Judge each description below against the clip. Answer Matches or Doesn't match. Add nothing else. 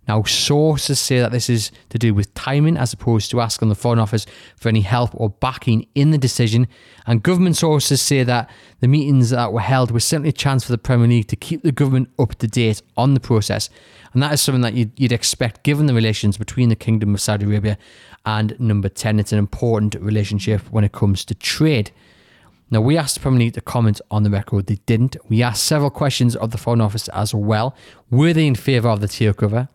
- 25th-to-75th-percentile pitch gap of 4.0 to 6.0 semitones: Doesn't match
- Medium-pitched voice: Doesn't match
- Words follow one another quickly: Matches